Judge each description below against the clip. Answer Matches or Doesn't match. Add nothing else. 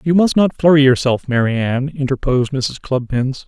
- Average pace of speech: Matches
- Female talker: Doesn't match